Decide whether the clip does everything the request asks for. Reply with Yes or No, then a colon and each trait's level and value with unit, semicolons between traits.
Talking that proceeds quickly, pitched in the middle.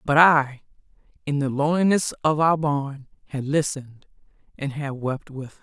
No: average, 160 wpm; medium, 145 Hz